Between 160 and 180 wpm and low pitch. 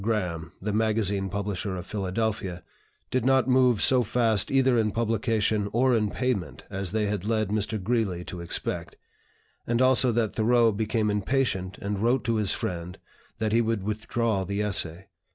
Yes: average, 165 wpm; low, 110 Hz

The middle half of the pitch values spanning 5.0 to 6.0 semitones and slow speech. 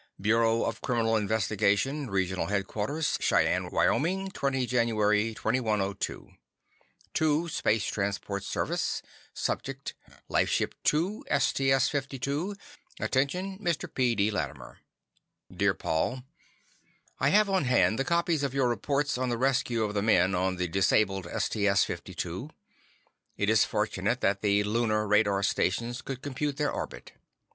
Yes: average, 5.3 semitones; slow, 130 wpm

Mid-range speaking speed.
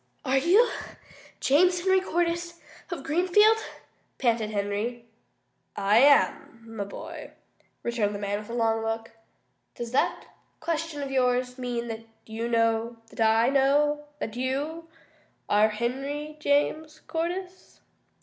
No: slow, 125 wpm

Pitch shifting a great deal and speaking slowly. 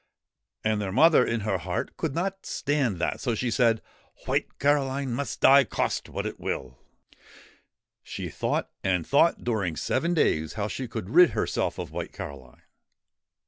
No: wide, 6.8 semitones; average, 165 wpm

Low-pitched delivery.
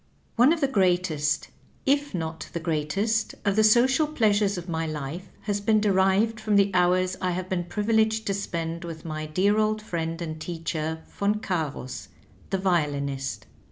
No: medium, 185 Hz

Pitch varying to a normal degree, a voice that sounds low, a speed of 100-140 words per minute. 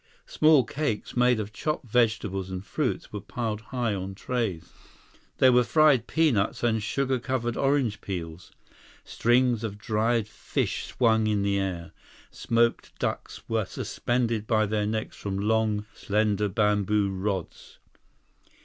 Yes: average, 3.1 semitones; low, 110 Hz; slow, 135 wpm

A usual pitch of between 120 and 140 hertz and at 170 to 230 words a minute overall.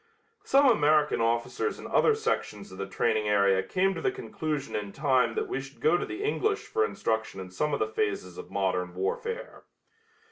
Yes: low, 135 Hz; average, 190 wpm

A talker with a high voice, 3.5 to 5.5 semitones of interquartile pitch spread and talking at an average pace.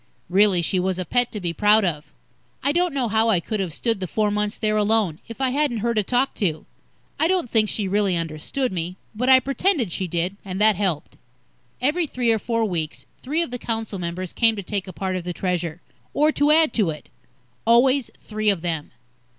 No: high, 210 Hz; average, 5.1 semitones; fast, 220 wpm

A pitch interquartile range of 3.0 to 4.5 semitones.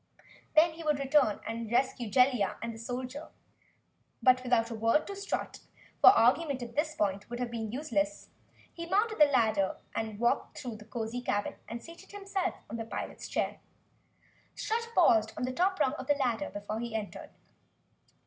No: average, 5.1 semitones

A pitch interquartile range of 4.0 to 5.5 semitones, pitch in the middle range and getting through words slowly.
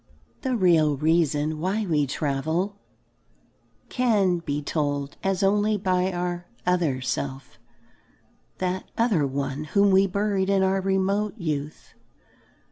Yes: average, 4.6 semitones; medium, 180 Hz; slow, 120 wpm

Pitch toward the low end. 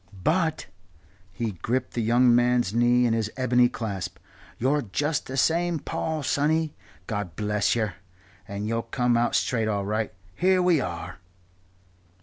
Yes: low, 120 Hz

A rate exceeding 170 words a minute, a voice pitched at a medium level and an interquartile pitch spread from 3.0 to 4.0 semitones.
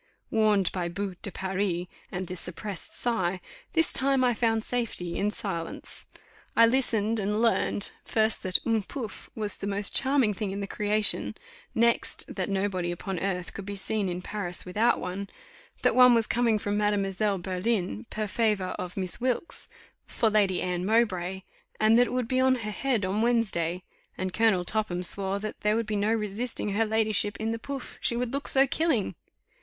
No: average, 180 wpm; high, 210 Hz; average, 3.3 semitones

